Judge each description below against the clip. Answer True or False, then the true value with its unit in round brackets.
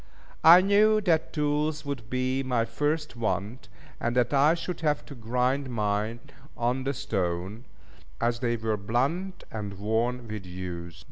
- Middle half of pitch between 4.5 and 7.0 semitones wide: True (5.3 semitones)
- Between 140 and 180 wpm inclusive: True (150 wpm)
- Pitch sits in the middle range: False (125 Hz)